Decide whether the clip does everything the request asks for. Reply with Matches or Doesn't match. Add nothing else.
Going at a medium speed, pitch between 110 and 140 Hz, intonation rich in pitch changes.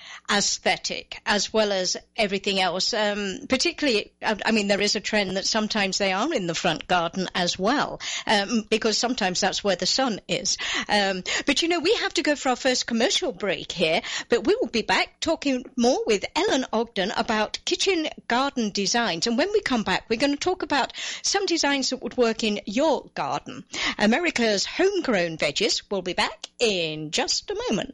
Doesn't match